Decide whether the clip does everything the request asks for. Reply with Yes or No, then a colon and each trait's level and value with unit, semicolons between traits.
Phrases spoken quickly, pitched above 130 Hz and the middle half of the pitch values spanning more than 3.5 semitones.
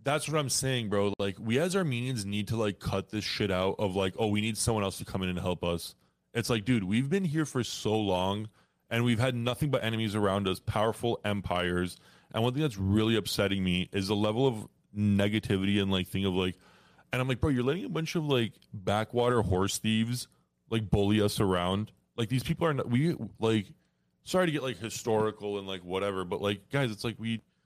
No: fast, 220 wpm; low, 110 Hz; average, 3.9 semitones